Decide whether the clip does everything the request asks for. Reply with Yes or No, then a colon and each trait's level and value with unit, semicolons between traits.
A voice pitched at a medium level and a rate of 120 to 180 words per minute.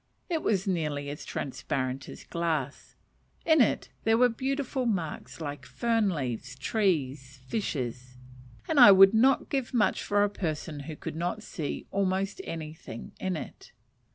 Yes: medium, 175 Hz; average, 150 wpm